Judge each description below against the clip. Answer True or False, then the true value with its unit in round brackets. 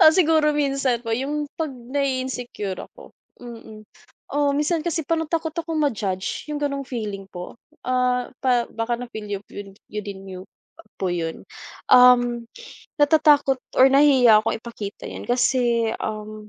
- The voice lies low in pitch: False (250 Hz)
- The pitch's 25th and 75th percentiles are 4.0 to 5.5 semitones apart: True (4.9 semitones)